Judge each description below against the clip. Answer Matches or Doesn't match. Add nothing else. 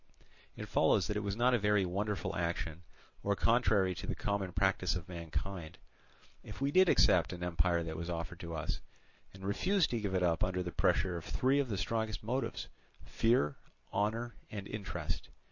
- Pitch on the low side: Matches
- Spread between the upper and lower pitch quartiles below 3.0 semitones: Doesn't match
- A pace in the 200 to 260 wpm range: Doesn't match